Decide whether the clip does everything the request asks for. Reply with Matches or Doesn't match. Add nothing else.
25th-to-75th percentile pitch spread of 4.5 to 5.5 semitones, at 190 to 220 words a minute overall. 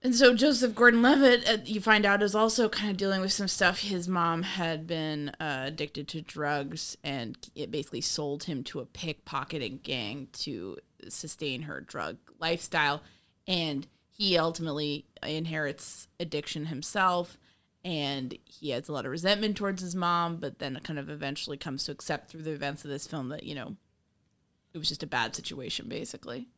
Doesn't match